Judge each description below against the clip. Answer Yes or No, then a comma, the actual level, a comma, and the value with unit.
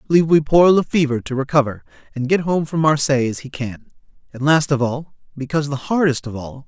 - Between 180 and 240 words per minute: Yes, average, 200 wpm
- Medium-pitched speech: Yes, medium, 145 Hz